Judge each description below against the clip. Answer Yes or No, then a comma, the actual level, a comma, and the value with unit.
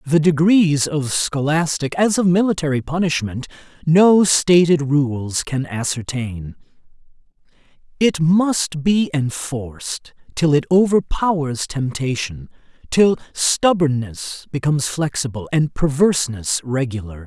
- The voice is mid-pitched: Yes, medium, 150 Hz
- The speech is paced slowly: Yes, slow, 95 wpm